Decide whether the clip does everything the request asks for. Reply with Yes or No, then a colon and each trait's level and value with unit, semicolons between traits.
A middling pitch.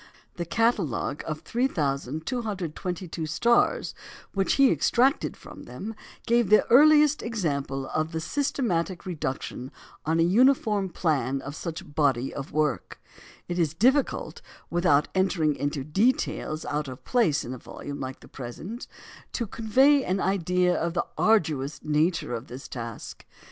Yes: medium, 170 Hz